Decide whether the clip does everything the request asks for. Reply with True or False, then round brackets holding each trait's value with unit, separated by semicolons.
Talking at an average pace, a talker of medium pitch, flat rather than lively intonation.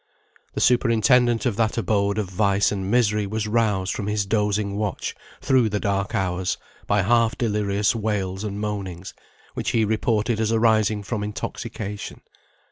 False (150 wpm; 105 Hz; 1.8 semitones)